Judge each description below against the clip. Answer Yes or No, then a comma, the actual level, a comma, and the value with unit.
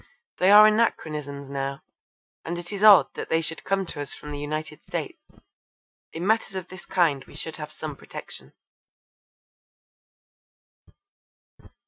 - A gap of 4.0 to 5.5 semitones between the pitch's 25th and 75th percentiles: Yes, average, 4.7 semitones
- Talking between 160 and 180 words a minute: No, average, 140 wpm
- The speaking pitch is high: No, medium, 165 Hz